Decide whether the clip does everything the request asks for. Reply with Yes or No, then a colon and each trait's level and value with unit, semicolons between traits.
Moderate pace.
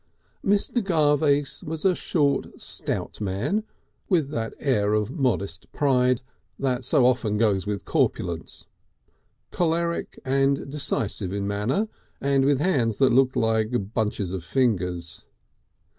No: slow, 125 wpm